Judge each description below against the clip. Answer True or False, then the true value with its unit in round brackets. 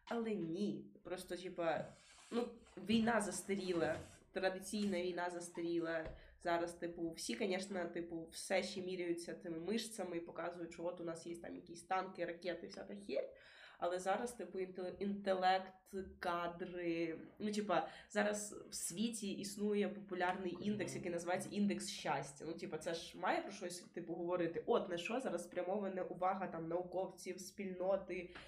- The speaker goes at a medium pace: True (145 wpm)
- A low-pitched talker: False (180 Hz)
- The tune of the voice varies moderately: False (2.1 semitones)